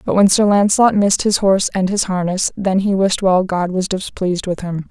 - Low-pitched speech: No, high, 190 Hz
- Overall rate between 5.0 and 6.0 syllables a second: Yes, 5.5 syllables/s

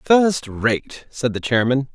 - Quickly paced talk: No, average, 155 wpm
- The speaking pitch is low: Yes, low, 130 Hz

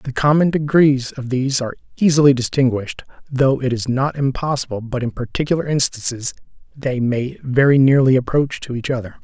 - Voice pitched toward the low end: Yes, low, 130 Hz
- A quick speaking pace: No, average, 165 wpm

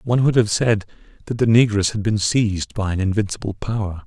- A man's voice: Yes, male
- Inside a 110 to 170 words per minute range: No, fast, 205 wpm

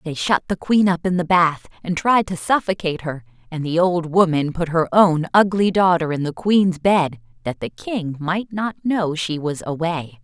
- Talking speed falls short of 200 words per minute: No, fast, 205 wpm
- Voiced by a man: No, female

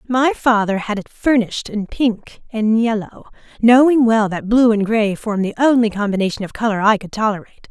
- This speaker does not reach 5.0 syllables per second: No, 5.5 syllables/s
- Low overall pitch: No, high, 220 Hz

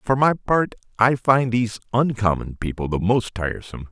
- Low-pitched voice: Yes, low, 115 Hz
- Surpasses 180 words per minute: No, average, 170 wpm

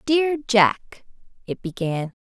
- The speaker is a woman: Yes, female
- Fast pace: No, slow, 110 wpm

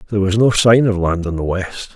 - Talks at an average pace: No, fast, 275 wpm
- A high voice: No, low, 100 Hz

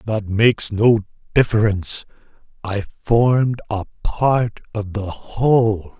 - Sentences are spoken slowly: Yes, slow, 110 wpm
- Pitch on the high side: No, low, 110 Hz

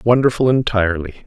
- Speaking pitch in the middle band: No, low, 110 Hz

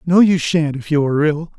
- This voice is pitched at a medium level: Yes, medium, 155 Hz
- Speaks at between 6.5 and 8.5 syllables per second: No, 5.6 syllables/s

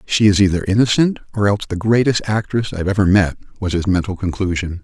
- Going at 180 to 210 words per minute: Yes, average, 200 wpm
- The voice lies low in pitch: Yes, low, 100 Hz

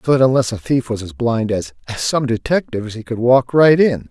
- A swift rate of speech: Yes, fast, 235 wpm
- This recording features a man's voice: Yes, male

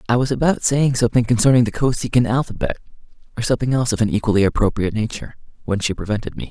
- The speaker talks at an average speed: Yes, average, 195 wpm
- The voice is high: No, low, 115 Hz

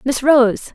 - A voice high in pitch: Yes, very high, 260 Hz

